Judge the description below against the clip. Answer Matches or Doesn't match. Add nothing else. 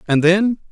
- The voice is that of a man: Matches